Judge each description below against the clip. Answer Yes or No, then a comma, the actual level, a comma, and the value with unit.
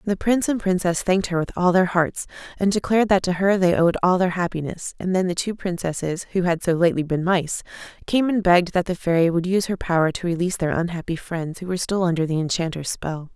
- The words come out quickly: Yes, fast, 240 wpm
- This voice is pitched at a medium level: Yes, medium, 180 Hz